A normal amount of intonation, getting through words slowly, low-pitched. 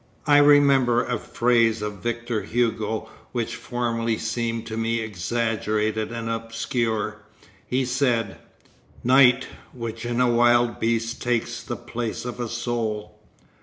No: narrow, 1.5 semitones; slow, 130 wpm; low, 115 Hz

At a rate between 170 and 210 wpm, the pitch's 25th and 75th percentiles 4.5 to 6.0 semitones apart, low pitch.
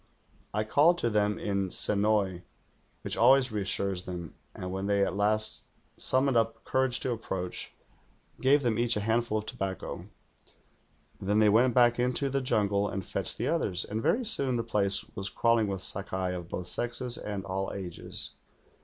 No: average, 175 wpm; average, 3.7 semitones; low, 105 Hz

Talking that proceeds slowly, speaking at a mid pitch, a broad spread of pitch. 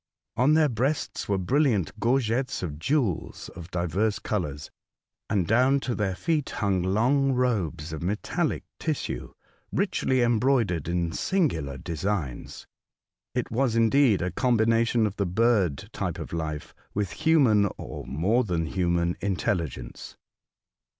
No: slow, 130 wpm; low, 105 Hz; wide, 6.6 semitones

